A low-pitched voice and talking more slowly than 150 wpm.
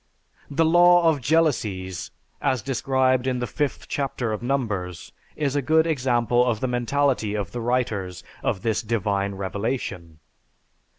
Yes: low, 125 Hz; average, 140 wpm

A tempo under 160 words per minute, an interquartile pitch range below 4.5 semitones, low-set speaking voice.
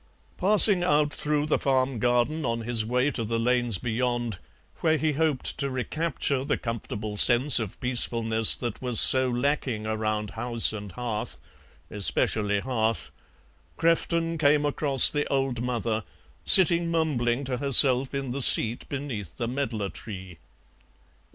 Yes: average, 140 wpm; average, 4.1 semitones; low, 125 Hz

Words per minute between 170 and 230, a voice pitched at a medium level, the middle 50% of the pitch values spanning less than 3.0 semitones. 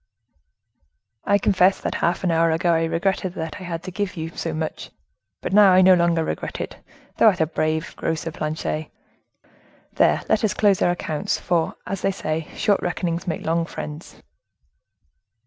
Yes: average, 175 wpm; medium, 170 Hz; narrow, 2.5 semitones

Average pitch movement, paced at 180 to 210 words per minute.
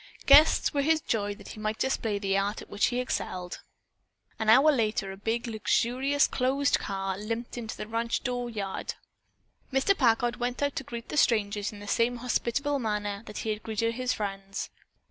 Yes: average, 3.4 semitones; average, 185 wpm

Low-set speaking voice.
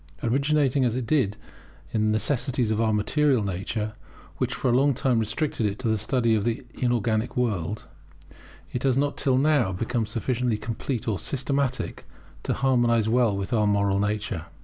Yes: low, 115 Hz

